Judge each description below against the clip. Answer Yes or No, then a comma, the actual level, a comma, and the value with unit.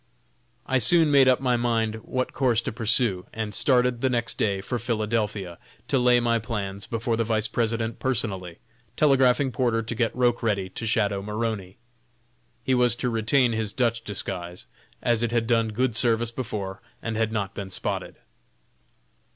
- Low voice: Yes, low, 115 Hz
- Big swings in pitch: No, narrow, 2.4 semitones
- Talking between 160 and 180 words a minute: Yes, average, 165 wpm